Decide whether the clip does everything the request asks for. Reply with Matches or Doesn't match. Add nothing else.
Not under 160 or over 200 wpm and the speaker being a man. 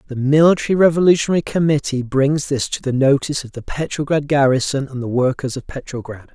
Matches